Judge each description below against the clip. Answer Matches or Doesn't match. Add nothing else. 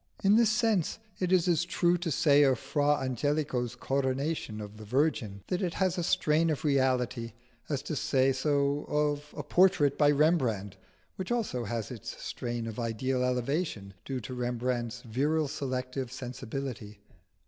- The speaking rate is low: Doesn't match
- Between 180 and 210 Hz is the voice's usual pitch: Doesn't match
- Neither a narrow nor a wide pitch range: Matches